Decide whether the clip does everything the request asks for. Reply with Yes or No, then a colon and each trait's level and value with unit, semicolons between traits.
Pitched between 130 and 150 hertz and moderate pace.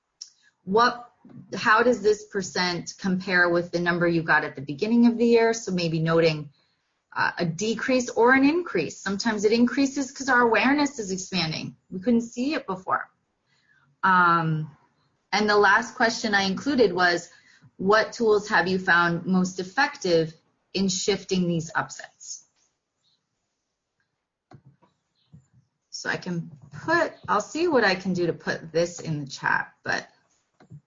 No: high, 190 Hz; average, 145 wpm